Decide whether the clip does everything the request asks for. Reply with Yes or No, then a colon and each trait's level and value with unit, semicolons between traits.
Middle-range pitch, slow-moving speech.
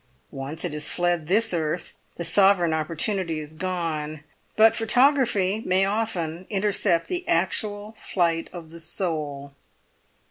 Yes: medium, 175 Hz; slow, 130 wpm